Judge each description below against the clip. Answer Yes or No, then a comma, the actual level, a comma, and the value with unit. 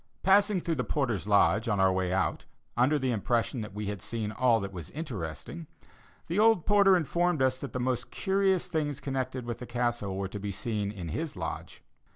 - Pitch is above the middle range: No, low, 125 Hz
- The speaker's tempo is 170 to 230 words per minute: Yes, average, 200 wpm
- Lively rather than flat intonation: Yes, wide, 7.1 semitones